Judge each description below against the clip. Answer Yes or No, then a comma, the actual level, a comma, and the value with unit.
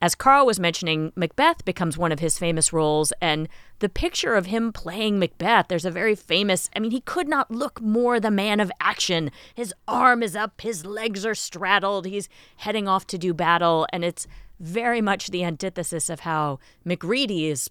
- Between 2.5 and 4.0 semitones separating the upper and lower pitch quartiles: No, average, 4.7 semitones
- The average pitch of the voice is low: No, high, 190 Hz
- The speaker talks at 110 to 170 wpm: No, average, 195 wpm